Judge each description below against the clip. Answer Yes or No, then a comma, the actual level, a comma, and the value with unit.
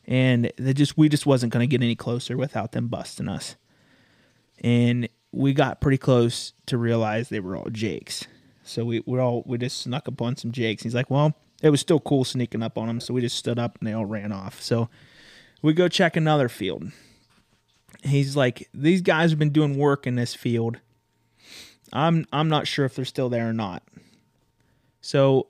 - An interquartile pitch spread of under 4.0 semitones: Yes, average, 3.3 semitones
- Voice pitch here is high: No, low, 125 Hz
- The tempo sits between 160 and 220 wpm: Yes, average, 200 wpm